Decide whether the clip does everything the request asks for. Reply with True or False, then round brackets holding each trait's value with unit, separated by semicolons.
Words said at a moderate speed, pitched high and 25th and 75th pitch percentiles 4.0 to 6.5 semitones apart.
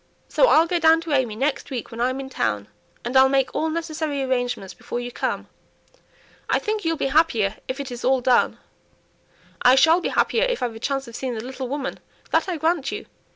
False (215 wpm; 270 Hz; 4.6 semitones)